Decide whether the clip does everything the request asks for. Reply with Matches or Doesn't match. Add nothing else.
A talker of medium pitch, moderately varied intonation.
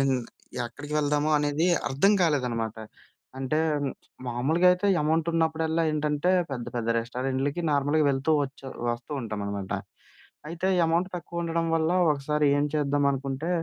Matches